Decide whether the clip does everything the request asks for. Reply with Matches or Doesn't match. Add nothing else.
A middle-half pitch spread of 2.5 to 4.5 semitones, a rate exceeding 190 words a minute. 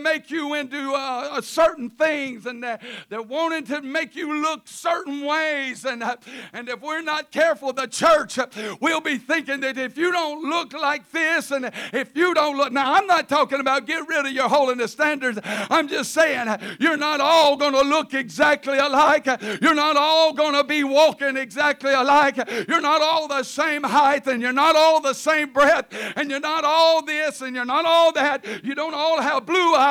Matches